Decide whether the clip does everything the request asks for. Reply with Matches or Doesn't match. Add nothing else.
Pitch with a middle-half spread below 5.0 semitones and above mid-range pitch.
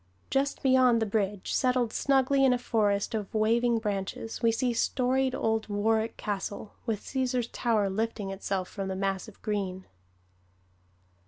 Matches